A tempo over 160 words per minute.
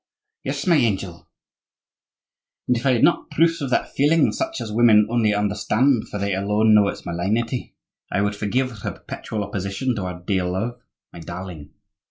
Yes: average, 175 wpm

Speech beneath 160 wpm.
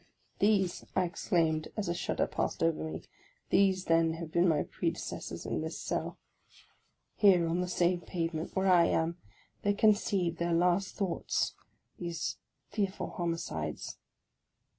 Yes: average, 150 wpm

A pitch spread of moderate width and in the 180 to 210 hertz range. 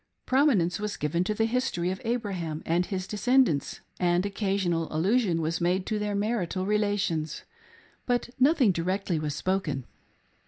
Yes: average, 3.9 semitones; high, 190 Hz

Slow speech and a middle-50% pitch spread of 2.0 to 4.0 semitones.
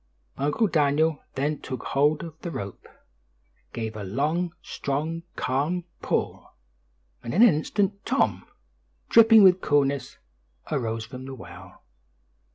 No: slow, 125 wpm; average, 4.7 semitones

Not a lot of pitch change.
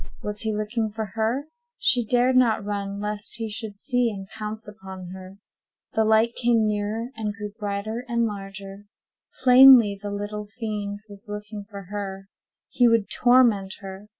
Yes: narrow, 2.1 semitones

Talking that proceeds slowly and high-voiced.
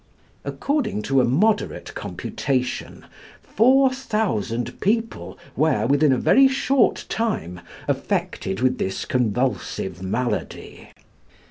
No: slow, 95 wpm; low, 135 Hz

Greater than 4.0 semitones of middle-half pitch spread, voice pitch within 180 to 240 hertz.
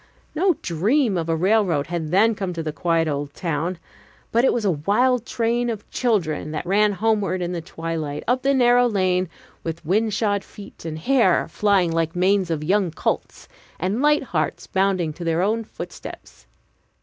Yes: average, 5.2 semitones; high, 190 Hz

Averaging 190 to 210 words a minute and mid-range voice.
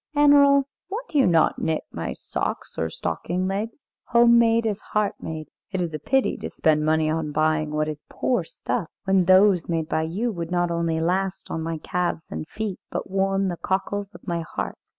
Yes: average, 200 wpm; medium, 180 Hz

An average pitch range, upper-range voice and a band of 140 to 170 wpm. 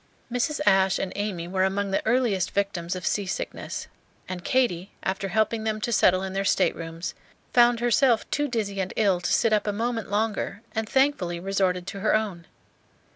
No: average, 3.1 semitones; high, 200 Hz; average, 180 wpm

